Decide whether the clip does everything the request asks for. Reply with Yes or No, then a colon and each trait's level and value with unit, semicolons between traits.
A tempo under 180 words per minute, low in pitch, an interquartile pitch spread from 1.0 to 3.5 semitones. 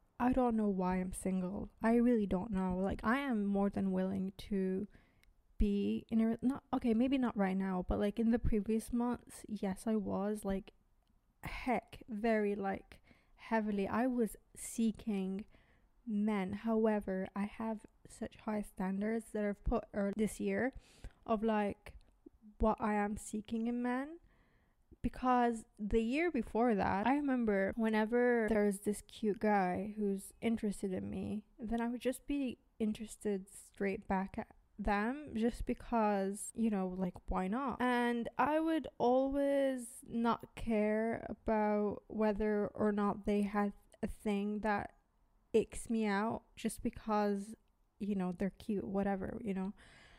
No: average, 150 wpm; high, 215 Hz; narrow, 2.5 semitones